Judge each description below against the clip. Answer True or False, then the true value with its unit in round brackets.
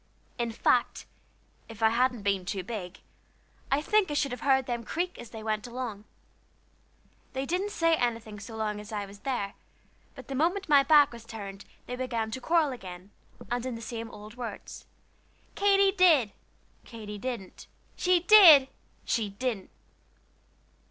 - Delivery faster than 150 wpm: True (160 wpm)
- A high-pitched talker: True (240 Hz)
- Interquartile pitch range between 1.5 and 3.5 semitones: False (4.9 semitones)